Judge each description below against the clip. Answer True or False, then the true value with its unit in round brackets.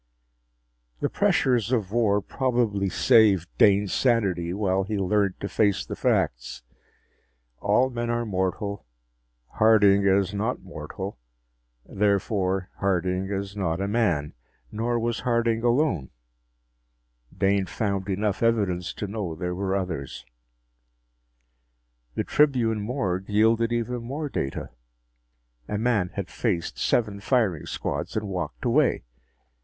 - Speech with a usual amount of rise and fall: True (3.5 semitones)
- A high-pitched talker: False (100 Hz)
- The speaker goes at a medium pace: False (120 wpm)